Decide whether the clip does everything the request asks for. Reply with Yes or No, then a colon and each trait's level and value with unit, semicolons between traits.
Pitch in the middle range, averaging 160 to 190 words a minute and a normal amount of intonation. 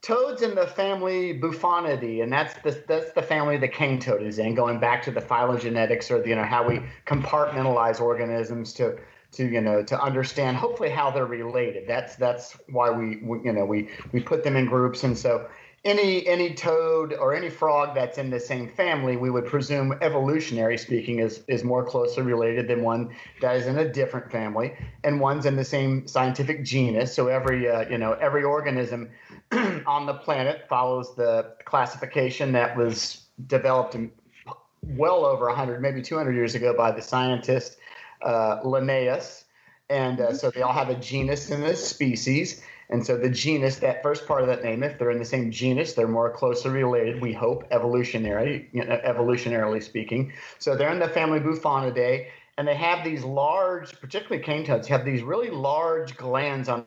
No: low, 130 Hz; average, 185 wpm; average, 3.8 semitones